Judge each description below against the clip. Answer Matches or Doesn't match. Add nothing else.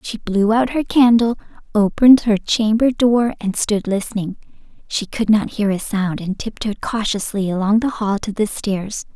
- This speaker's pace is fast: Doesn't match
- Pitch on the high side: Matches